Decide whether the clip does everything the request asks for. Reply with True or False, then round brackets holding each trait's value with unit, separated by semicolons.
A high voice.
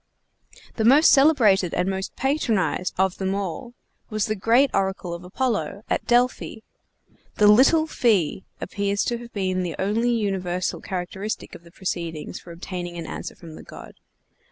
True (195 Hz)